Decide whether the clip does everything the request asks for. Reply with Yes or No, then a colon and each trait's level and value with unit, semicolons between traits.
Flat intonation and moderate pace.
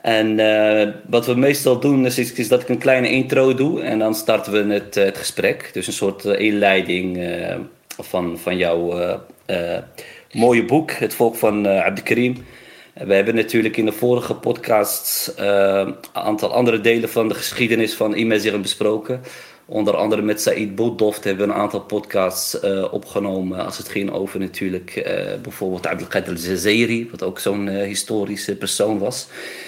No: average, 3.0 semitones; average, 170 wpm